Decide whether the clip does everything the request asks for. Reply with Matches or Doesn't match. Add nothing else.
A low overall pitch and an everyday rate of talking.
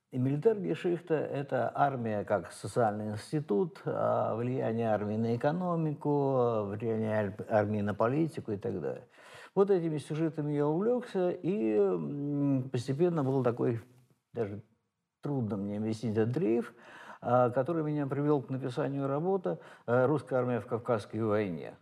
Matches